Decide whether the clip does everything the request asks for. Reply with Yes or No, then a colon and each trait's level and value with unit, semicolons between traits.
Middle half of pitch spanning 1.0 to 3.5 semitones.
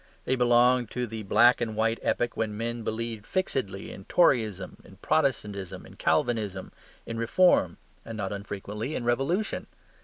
Yes: average, 3.1 semitones